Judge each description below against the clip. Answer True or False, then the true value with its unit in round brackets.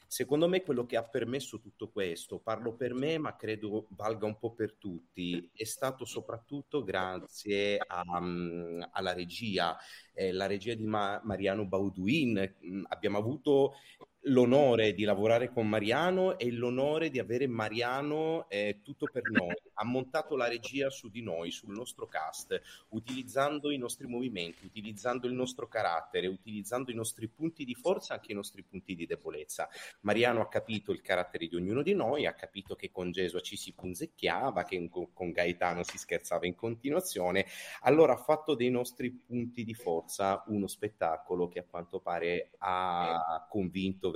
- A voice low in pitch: True (110 Hz)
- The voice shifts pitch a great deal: False (4.8 semitones)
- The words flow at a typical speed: True (160 wpm)